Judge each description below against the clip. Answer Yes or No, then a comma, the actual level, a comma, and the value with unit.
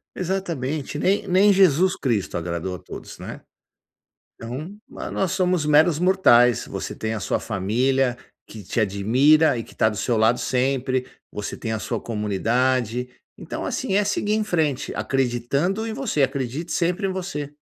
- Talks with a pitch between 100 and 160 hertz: Yes, low, 135 Hz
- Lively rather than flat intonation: Yes, wide, 7.4 semitones